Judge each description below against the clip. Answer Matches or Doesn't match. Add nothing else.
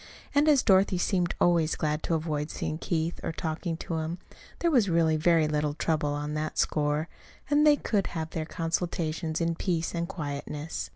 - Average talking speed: Matches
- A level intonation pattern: Matches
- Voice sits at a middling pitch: Matches